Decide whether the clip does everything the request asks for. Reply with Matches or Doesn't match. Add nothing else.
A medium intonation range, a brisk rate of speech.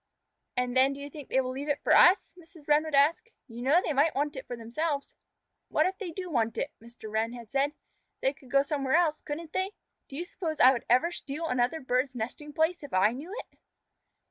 Matches